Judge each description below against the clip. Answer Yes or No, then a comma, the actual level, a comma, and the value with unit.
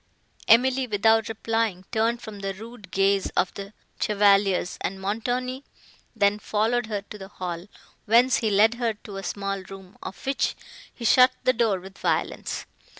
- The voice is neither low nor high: No, high, 210 Hz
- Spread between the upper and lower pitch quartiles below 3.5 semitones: Yes, average, 2.8 semitones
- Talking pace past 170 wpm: No, average, 160 wpm